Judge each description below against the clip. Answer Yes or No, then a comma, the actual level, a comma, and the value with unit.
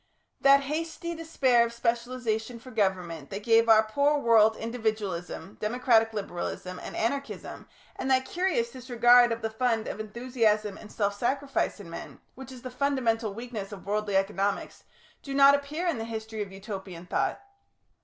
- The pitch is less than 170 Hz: No, high, 230 Hz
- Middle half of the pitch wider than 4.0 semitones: No, average, 3.5 semitones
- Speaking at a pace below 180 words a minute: Yes, average, 160 wpm